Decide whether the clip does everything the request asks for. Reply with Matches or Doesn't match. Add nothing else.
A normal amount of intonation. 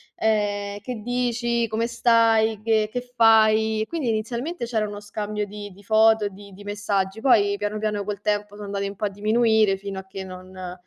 Doesn't match